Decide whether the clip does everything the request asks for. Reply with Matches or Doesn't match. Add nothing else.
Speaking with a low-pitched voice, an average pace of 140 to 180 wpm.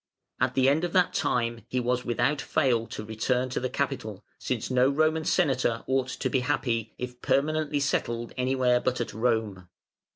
Matches